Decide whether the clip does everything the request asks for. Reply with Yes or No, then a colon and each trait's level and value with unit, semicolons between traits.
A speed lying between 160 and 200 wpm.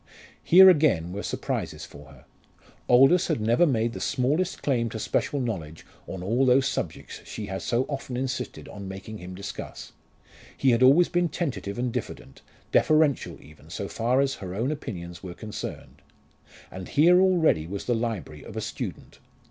Yes: average, 170 wpm